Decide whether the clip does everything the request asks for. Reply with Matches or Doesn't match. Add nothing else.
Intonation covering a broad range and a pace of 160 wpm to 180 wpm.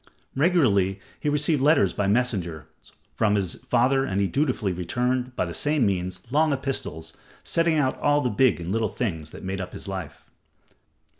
Matches